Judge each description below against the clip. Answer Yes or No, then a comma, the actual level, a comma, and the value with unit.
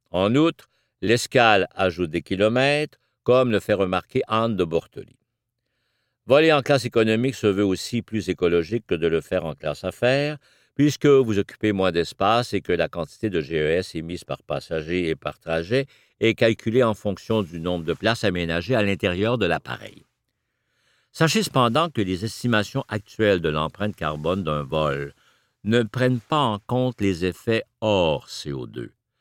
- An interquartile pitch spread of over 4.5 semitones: Yes, average, 5.3 semitones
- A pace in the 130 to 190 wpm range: Yes, average, 160 wpm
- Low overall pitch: Yes, low, 110 Hz